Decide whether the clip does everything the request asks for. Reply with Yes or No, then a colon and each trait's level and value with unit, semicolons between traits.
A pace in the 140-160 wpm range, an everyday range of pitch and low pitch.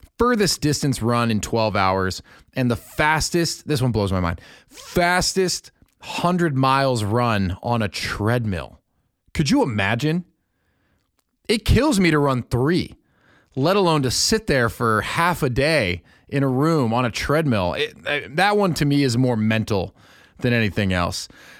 No: average, 155 wpm; wide, 6.4 semitones; low, 125 Hz